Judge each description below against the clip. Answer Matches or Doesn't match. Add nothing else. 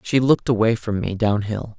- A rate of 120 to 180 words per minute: Doesn't match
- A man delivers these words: Matches